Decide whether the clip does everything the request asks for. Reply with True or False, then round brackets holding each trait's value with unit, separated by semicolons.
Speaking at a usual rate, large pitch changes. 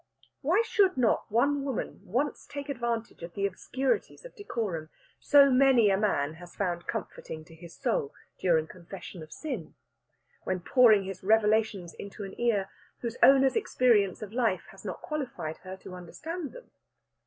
True (160 wpm; 6.5 semitones)